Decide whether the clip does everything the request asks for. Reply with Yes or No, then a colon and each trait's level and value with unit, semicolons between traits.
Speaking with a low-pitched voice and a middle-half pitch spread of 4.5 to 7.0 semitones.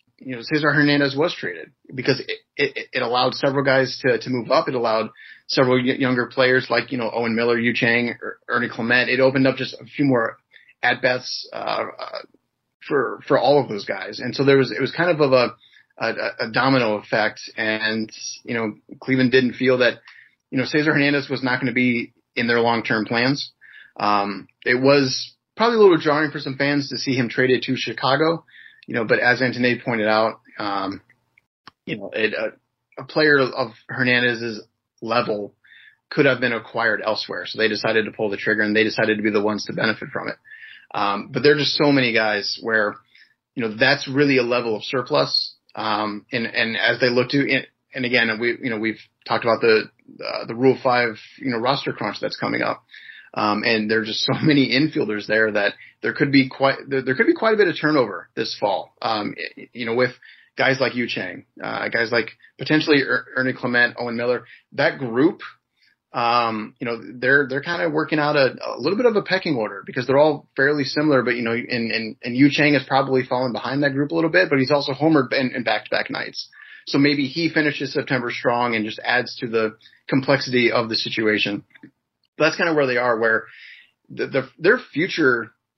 No: low, 125 Hz; average, 3.5 semitones